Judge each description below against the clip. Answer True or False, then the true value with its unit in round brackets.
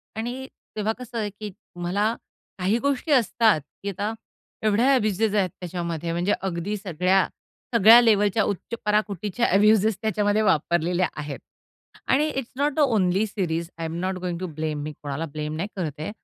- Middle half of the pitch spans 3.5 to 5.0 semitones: True (4.2 semitones)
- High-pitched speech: True (200 Hz)